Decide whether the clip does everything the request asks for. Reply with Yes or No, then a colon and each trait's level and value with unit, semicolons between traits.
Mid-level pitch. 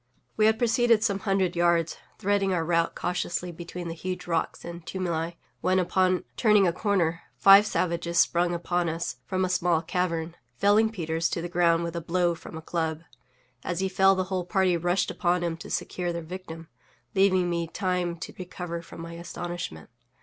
Yes: medium, 175 Hz